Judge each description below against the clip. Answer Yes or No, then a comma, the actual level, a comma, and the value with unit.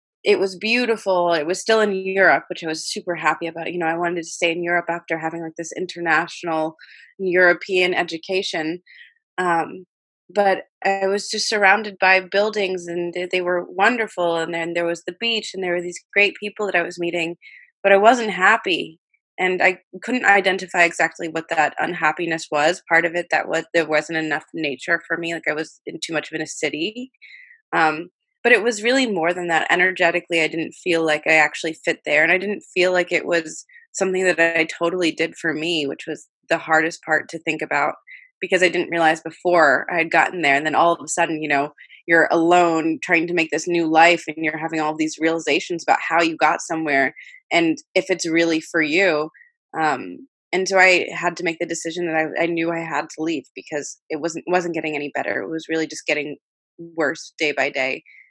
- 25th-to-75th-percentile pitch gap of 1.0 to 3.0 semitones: Yes, average, 2.7 semitones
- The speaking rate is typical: No, fast, 210 wpm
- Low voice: No, medium, 170 Hz